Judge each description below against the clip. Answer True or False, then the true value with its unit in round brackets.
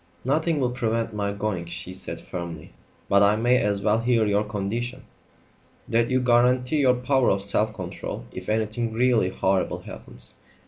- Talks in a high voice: False (110 Hz)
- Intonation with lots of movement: False (3.6 semitones)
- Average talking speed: True (165 wpm)